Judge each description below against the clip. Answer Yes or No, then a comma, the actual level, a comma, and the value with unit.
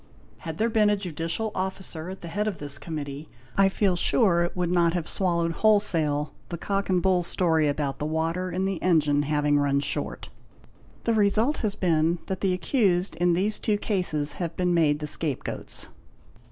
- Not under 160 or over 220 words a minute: Yes, average, 190 wpm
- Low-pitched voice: No, medium, 175 Hz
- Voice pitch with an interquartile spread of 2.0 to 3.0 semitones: No, average, 3.7 semitones